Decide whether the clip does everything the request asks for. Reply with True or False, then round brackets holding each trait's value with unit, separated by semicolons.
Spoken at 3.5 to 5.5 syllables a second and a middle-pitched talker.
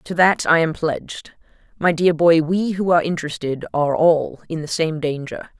True (5.1 syllables/s; 160 Hz)